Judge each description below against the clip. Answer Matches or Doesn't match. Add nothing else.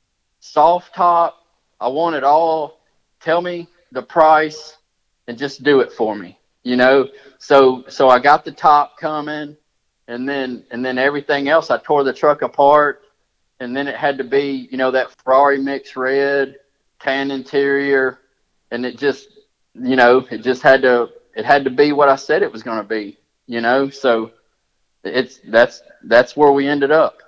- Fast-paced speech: Doesn't match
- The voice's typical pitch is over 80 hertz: Matches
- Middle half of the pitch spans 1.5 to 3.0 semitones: Matches